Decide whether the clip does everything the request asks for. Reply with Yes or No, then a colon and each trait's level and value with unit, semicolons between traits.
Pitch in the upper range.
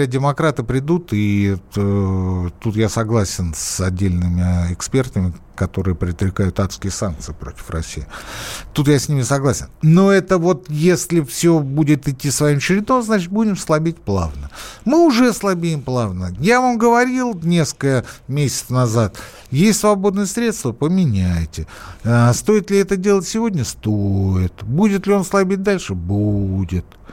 No: low, 130 Hz